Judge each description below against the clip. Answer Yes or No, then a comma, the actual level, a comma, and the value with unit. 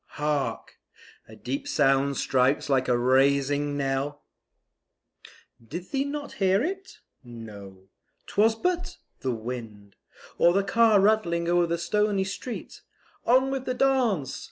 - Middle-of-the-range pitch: Yes, medium, 165 Hz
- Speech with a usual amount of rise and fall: No, wide, 8.6 semitones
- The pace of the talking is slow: Yes, slow, 130 wpm